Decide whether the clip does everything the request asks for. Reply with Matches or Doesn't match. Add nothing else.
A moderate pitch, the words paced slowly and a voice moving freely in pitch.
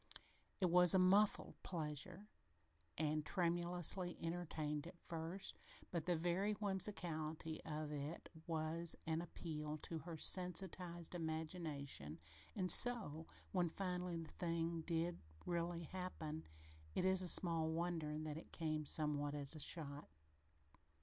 Doesn't match